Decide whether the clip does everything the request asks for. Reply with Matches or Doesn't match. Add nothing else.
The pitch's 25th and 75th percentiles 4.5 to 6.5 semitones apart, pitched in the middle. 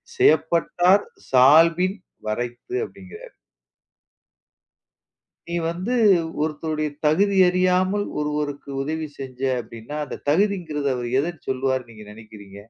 Matches